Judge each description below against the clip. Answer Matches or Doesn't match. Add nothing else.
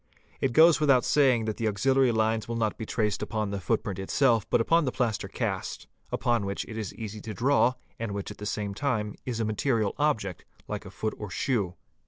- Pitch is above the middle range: Doesn't match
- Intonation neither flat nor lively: Matches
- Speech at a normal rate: Doesn't match